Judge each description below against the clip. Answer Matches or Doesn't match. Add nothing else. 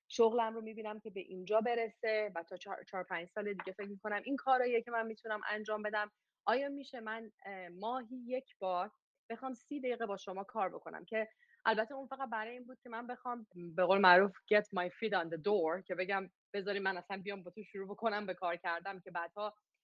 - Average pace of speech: Doesn't match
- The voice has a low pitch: Doesn't match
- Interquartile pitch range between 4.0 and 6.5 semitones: Doesn't match